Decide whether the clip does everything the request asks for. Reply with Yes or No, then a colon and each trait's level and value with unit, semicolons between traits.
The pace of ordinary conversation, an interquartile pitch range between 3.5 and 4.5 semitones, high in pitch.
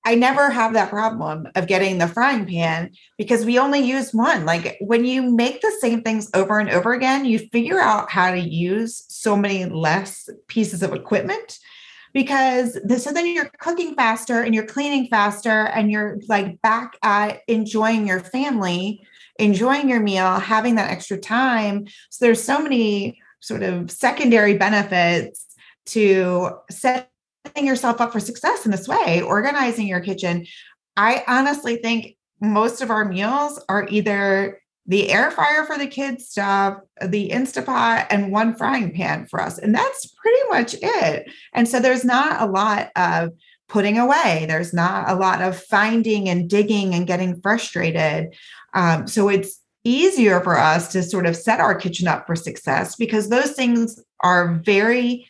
Yes: average, 165 wpm; average, 4.2 semitones; high, 215 Hz